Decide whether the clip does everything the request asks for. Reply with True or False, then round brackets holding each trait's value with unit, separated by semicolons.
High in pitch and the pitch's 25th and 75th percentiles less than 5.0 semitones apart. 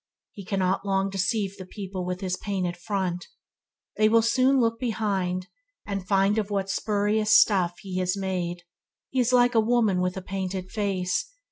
True (195 Hz; 2.8 semitones)